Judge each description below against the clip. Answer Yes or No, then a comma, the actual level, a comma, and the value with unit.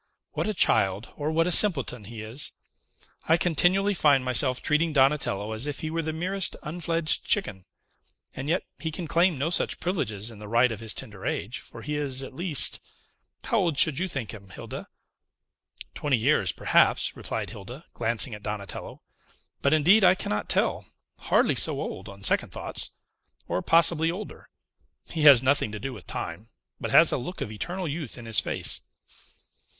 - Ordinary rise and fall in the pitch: No, wide, 6.9 semitones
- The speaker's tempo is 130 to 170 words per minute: No, average, 180 wpm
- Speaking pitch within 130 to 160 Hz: Yes, medium, 140 Hz